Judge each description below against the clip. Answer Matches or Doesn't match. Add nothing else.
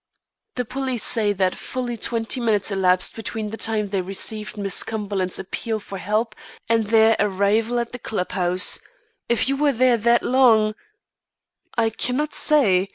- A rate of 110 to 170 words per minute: Matches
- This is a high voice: Matches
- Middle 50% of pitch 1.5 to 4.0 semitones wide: Matches